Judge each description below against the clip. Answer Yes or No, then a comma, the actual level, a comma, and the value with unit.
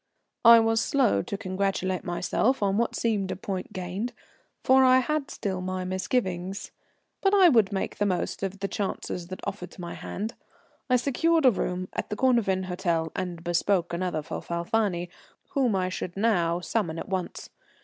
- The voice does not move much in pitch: No, average, 4.1 semitones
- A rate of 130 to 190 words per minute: Yes, average, 175 wpm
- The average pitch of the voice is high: Yes, high, 195 Hz